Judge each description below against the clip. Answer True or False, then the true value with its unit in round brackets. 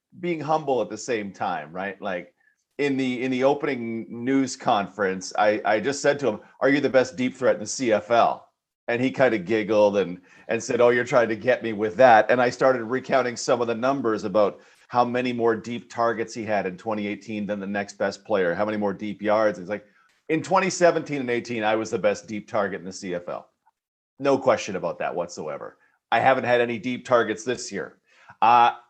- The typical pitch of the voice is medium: False (120 Hz)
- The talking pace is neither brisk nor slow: False (215 wpm)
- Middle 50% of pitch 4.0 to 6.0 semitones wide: False (3.6 semitones)